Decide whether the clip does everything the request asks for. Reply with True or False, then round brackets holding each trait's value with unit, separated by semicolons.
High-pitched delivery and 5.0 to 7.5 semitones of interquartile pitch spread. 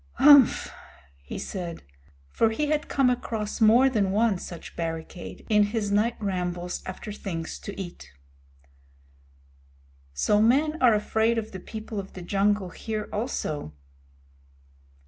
False (210 Hz; 4.0 semitones)